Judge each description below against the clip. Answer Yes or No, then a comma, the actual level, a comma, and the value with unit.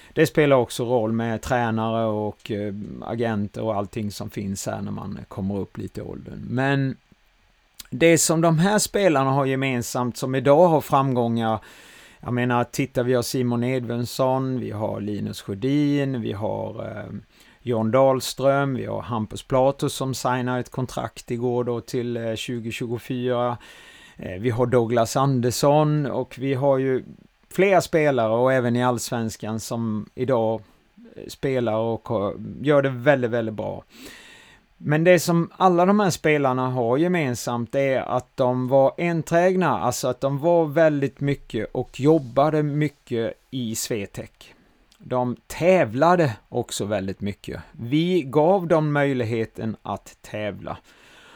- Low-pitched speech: Yes, low, 125 Hz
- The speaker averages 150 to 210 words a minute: No, average, 140 wpm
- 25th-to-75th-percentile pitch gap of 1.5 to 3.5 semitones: No, average, 3.9 semitones